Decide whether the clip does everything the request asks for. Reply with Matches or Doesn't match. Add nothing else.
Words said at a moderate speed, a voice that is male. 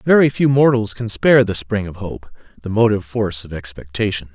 Matches